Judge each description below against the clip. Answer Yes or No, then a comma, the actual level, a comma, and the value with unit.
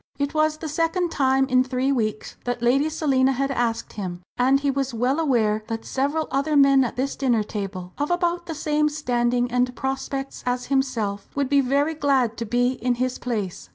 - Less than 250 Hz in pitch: No, very high, 265 Hz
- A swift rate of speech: No, average, 195 wpm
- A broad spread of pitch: No, average, 2.8 semitones